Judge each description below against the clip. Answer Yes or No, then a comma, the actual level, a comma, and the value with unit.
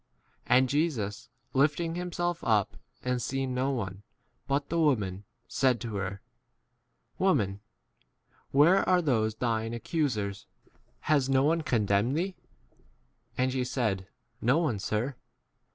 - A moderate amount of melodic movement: No, wide, 5.7 semitones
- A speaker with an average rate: No, slow, 130 wpm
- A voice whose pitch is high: No, low, 130 Hz